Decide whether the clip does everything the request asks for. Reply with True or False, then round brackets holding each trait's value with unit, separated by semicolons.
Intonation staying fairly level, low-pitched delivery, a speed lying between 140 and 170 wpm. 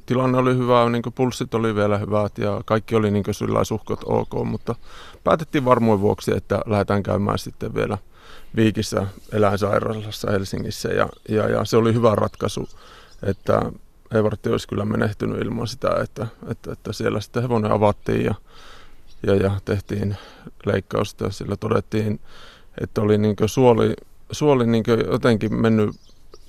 True (2.3 semitones; 110 Hz; 145 wpm)